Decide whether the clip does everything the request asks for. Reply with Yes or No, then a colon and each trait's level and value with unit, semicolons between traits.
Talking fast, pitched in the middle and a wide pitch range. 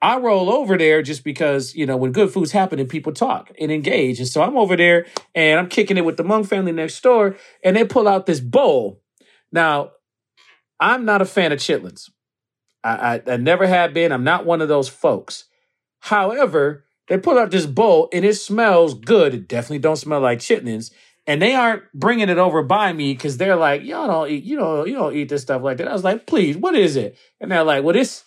Yes: fast, 225 wpm; medium, 170 Hz; wide, 5.7 semitones